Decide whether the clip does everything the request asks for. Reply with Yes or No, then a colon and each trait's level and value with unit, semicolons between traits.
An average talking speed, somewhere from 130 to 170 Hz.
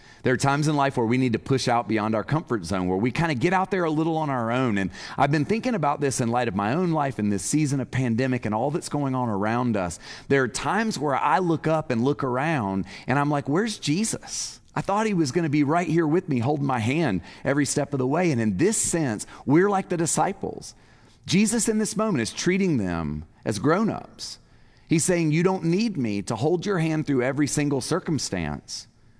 No: fast, 240 wpm; medium, 140 Hz